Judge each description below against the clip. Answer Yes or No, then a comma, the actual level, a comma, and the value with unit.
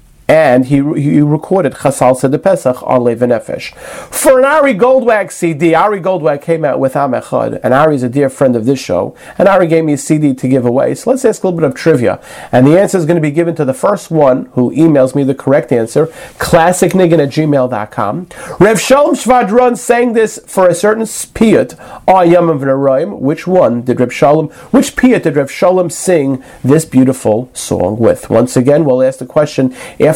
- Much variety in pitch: Yes, wide, 5.9 semitones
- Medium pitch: Yes, medium, 155 Hz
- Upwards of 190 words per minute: Yes, average, 200 wpm